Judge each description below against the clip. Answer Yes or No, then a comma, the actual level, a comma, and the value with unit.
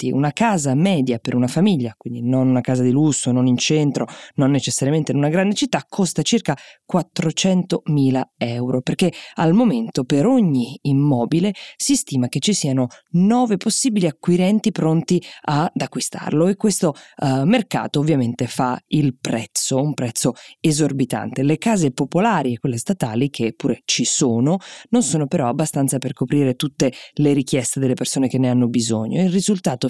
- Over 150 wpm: Yes, average, 165 wpm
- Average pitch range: No, wide, 5.8 semitones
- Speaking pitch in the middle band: Yes, medium, 145 Hz